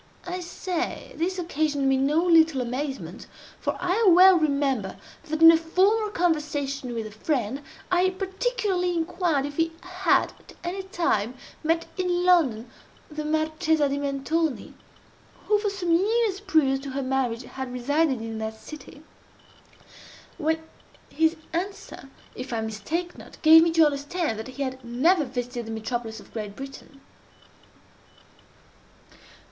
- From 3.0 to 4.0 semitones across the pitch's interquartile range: No, average, 5.1 semitones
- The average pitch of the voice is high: Yes, very high, 310 Hz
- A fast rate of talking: No, average, 140 wpm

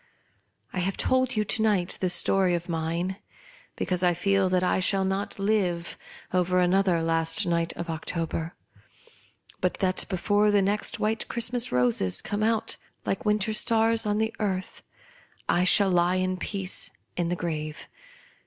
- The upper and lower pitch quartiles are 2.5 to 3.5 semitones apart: Yes, average, 3.2 semitones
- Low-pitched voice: No, medium, 185 Hz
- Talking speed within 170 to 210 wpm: No, average, 155 wpm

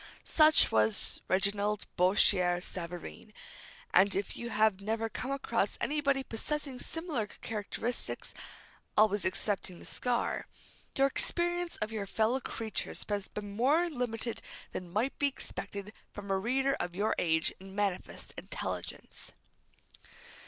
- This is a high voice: Yes, high, 215 Hz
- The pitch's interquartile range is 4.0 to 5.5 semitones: Yes, average, 5.1 semitones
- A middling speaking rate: No, slow, 125 wpm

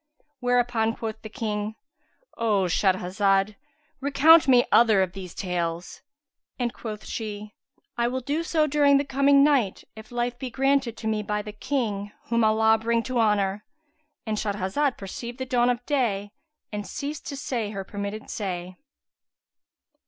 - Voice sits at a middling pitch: No, high, 225 Hz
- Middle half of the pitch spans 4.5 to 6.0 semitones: No, average, 4.1 semitones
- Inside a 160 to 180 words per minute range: No, average, 150 wpm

